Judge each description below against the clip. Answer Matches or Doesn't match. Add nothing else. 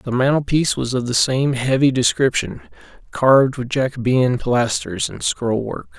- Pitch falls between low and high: Doesn't match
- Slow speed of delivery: Doesn't match